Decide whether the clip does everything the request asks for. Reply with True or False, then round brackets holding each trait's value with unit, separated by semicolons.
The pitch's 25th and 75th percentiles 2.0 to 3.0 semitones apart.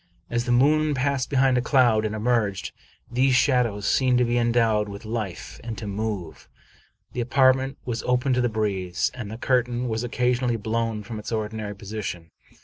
True (2.7 semitones)